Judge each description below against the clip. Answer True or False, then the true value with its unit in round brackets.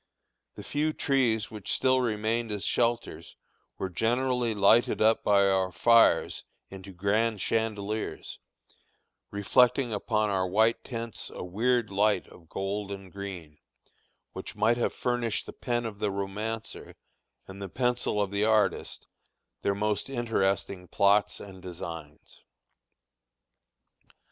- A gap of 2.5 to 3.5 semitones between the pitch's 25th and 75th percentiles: True (3.0 semitones)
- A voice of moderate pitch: False (105 Hz)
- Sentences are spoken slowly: True (125 wpm)